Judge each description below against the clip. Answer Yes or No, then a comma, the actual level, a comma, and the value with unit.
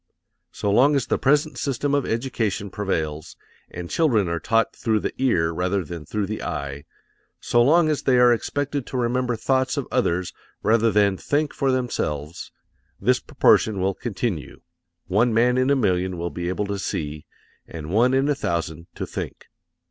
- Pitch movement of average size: No, wide, 6.4 semitones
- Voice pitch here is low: Yes, low, 110 Hz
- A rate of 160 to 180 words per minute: Yes, average, 175 wpm